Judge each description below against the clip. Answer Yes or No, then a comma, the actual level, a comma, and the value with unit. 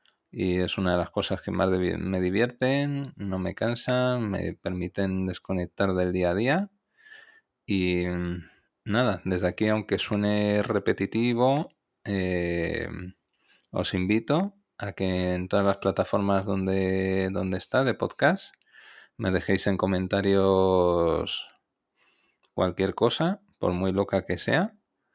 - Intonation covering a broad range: No, average, 3.6 semitones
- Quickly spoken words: No, slow, 125 wpm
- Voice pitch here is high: No, very low, 95 Hz